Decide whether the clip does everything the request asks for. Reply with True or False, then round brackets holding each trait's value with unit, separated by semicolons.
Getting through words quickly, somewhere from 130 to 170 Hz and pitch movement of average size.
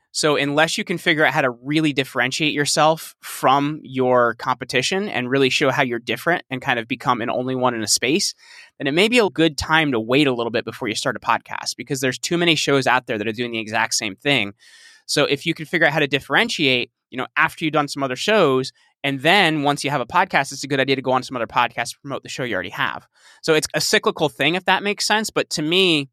True (260 wpm; 140 Hz; 4.0 semitones)